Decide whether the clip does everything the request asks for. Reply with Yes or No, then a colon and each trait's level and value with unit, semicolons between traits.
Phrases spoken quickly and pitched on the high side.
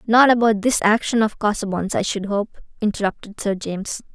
No: average, 175 wpm; high, 210 Hz